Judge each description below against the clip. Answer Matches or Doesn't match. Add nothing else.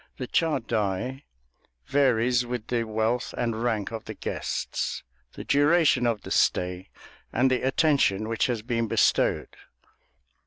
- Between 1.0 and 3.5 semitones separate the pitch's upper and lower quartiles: Matches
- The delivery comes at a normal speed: Doesn't match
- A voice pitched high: Doesn't match